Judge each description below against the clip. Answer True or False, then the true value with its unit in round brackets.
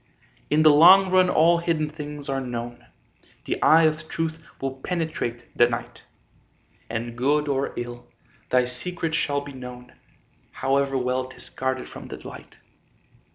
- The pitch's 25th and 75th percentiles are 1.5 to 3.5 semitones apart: False (4.1 semitones)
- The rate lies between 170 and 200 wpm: False (150 wpm)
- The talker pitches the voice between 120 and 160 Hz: True (140 Hz)